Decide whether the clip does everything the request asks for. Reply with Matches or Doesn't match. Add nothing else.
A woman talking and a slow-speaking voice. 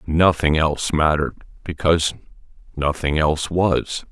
Doesn't match